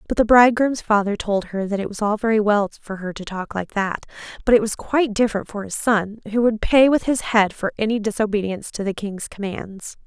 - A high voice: Yes, high, 210 Hz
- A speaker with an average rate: No, fast, 235 wpm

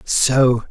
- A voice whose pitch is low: Yes, low, 125 Hz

